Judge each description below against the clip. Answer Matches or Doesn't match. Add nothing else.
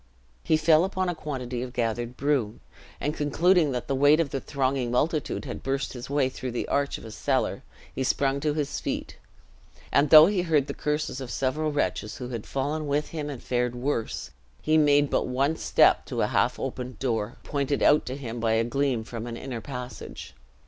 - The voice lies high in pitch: Doesn't match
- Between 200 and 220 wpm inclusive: Matches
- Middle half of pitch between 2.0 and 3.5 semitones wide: Matches